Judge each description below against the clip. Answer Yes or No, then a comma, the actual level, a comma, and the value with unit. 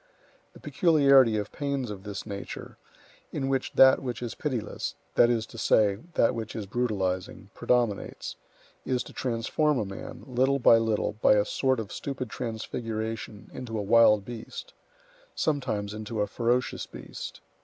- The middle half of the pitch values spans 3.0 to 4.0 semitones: Yes, average, 3.3 semitones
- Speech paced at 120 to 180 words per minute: Yes, average, 145 wpm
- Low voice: Yes, low, 115 Hz